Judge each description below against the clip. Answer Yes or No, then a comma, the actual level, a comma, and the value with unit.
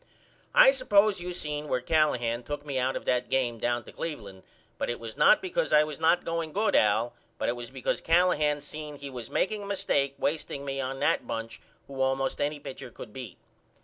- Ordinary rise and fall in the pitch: Yes, average, 4.6 semitones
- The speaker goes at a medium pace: No, fast, 210 wpm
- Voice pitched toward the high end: No, medium, 140 Hz